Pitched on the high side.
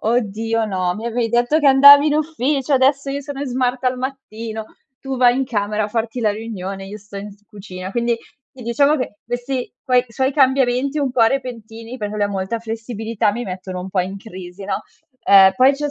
Yes: high, 230 Hz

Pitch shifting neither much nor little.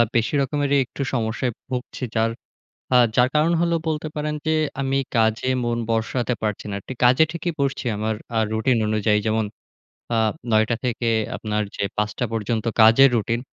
Yes: average, 3.7 semitones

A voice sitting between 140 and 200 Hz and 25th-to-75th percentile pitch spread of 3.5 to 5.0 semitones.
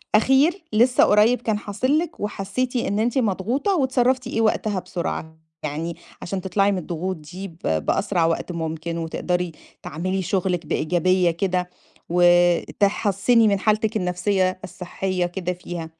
Yes: high, 190 Hz; average, 3.8 semitones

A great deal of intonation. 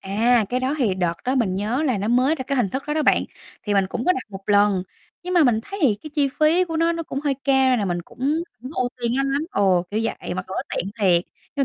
Yes: wide, 5.8 semitones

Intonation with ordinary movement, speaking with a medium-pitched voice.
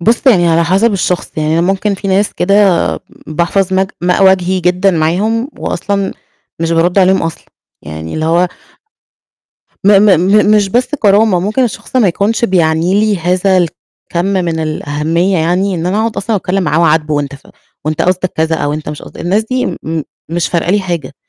Yes: average, 3.3 semitones; medium, 180 Hz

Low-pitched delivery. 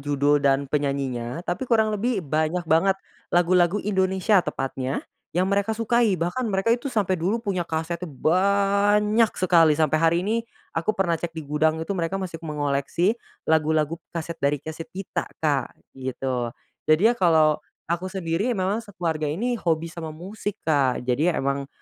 No: medium, 170 Hz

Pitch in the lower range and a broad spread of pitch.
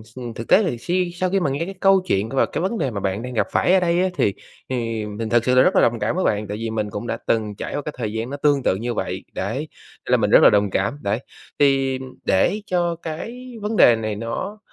Yes: low, 125 Hz; wide, 8.0 semitones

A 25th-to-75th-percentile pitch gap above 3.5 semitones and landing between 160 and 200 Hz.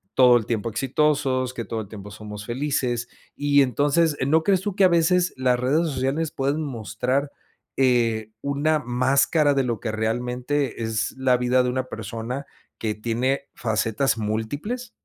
No: average, 3.9 semitones; low, 130 Hz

